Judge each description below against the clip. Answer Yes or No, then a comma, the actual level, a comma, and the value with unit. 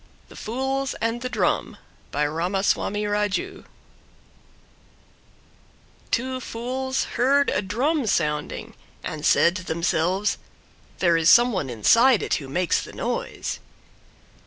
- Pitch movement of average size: No, wide, 7.1 semitones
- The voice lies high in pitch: Yes, high, 210 Hz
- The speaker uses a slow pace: Yes, slow, 115 wpm